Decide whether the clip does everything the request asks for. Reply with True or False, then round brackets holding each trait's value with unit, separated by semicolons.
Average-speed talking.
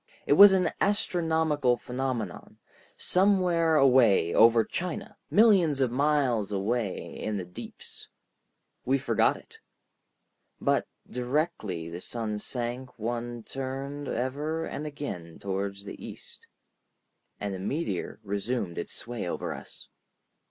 False (115 wpm)